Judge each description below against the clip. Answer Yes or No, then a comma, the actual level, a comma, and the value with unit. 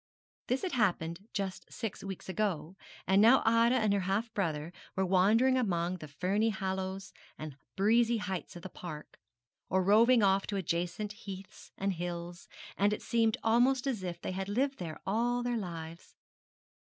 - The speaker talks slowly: No, average, 170 wpm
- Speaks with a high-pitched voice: Yes, high, 195 Hz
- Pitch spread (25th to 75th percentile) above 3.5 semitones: Yes, average, 4.0 semitones